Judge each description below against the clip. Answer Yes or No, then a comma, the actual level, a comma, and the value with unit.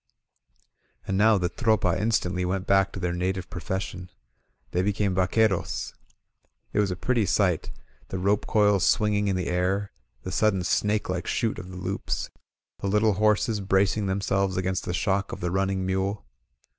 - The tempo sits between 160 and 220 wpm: Yes, average, 170 wpm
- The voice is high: No, very low, 95 Hz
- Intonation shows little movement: Yes, narrow, 2.0 semitones